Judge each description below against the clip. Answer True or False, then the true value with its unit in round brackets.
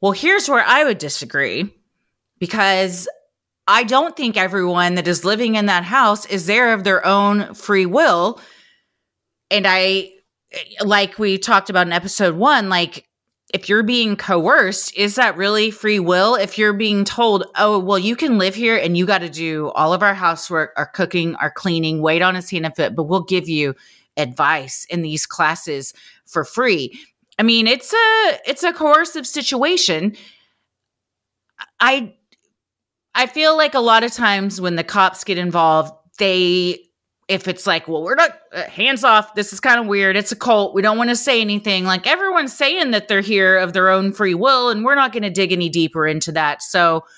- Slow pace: False (190 wpm)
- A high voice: True (195 Hz)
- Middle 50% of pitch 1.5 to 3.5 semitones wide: False (4.1 semitones)